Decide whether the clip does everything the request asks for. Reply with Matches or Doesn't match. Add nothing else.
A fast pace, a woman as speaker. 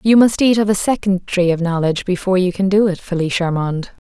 Matches